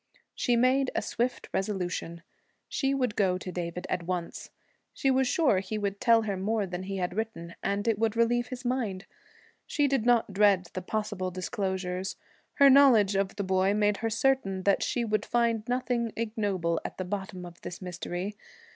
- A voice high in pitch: Yes, high, 205 Hz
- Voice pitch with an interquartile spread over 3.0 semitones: Yes, average, 4.0 semitones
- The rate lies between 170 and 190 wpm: Yes, average, 180 wpm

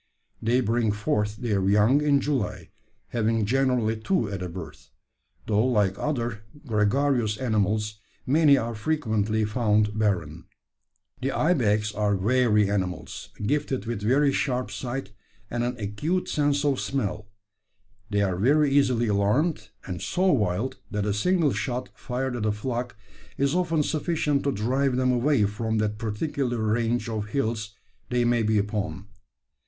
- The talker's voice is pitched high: No, low, 115 Hz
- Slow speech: No, average, 145 wpm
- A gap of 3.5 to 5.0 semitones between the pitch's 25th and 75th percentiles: Yes, average, 4.2 semitones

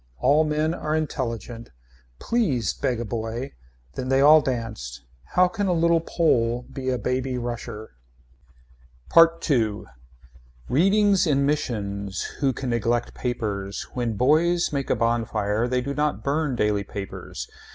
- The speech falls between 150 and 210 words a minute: No, average, 140 wpm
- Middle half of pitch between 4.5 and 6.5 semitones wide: Yes, average, 5.0 semitones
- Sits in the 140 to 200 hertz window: No, low, 125 Hz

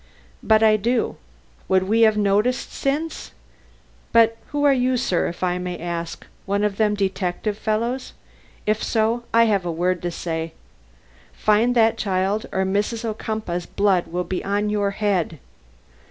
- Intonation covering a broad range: No, average, 3.5 semitones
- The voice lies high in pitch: Yes, high, 210 Hz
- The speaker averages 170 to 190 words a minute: No, average, 155 wpm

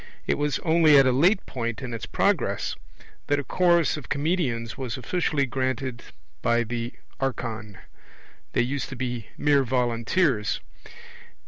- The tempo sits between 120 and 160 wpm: Yes, average, 140 wpm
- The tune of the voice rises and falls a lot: No, average, 3.7 semitones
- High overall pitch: No, low, 130 Hz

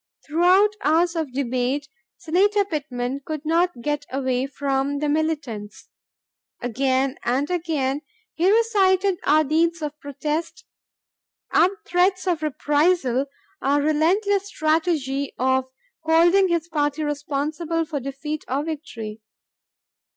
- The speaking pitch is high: Yes, very high, 300 Hz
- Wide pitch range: No, average, 3.7 semitones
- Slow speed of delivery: Yes, slow, 115 wpm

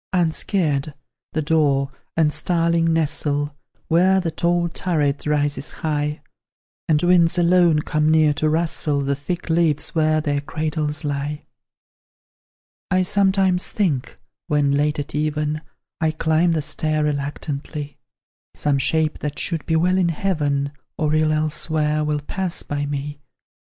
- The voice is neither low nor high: Yes, medium, 155 Hz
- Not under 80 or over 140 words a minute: Yes, slow, 135 wpm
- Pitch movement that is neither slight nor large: No, narrow, 2.2 semitones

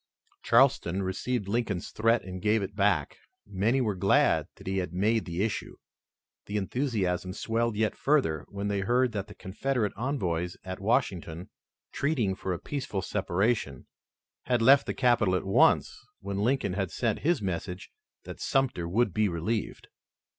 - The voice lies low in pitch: Yes, low, 100 Hz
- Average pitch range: Yes, average, 4.1 semitones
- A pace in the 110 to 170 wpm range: Yes, average, 155 wpm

